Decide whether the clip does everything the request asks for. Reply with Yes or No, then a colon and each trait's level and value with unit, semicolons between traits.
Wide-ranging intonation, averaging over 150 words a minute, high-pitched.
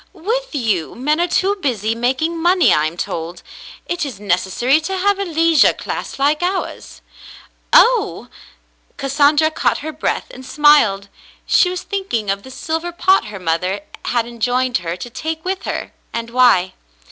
Yes: wide, 7.8 semitones; average, 160 wpm; very high, 275 Hz